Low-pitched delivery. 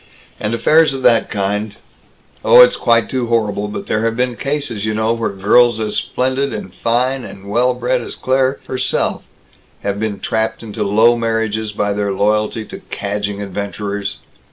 Yes: low, 110 Hz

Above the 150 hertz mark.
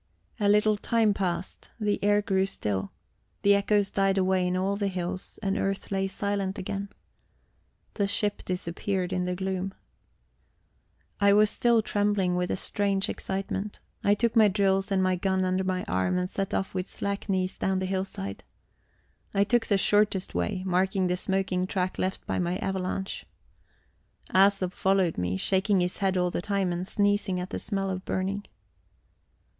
Yes: high, 190 Hz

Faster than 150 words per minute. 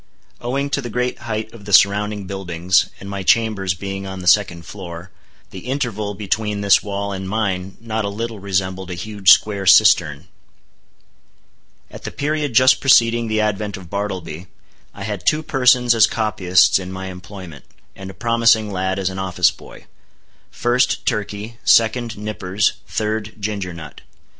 Yes: average, 160 wpm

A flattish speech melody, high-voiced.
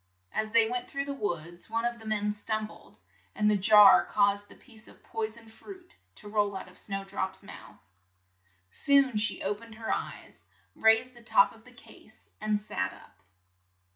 Yes: narrow, 2.0 semitones; high, 215 Hz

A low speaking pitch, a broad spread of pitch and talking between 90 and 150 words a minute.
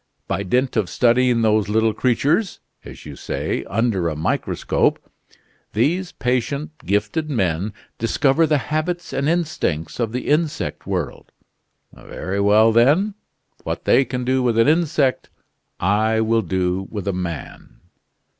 Yes: low, 115 Hz; wide, 5.9 semitones; slow, 135 wpm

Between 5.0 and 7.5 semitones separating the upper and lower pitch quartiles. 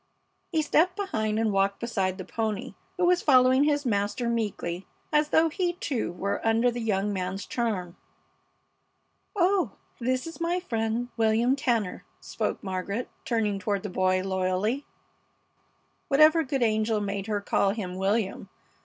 Yes: average, 5.3 semitones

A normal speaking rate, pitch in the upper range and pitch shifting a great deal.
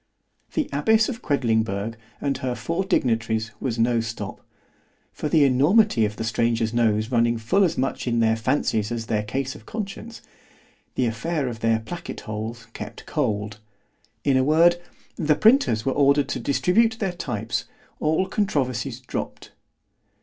No: average, 145 wpm; low, 125 Hz; wide, 5.9 semitones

